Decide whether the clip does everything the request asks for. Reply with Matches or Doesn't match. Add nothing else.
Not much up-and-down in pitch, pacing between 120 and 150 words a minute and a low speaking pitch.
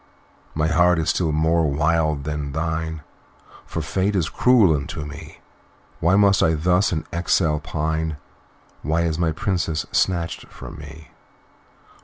Matches